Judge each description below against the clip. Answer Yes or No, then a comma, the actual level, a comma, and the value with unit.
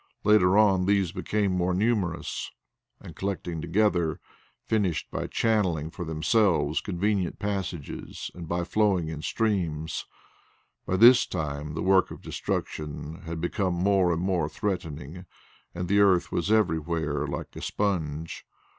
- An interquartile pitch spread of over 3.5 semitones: Yes, average, 3.9 semitones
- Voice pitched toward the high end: No, very low, 90 Hz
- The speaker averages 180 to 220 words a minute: No, slow, 135 wpm